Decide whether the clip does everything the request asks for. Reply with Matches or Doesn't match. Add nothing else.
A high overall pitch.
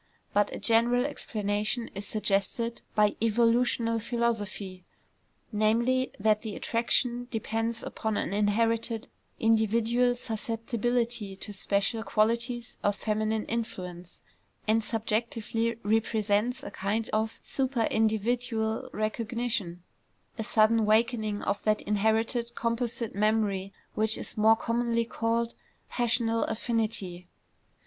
Matches